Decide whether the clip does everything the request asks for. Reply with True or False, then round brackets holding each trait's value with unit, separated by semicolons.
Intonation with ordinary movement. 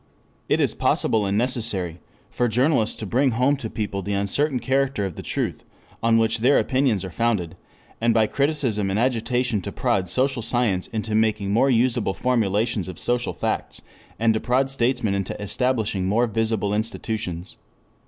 True (3.7 semitones)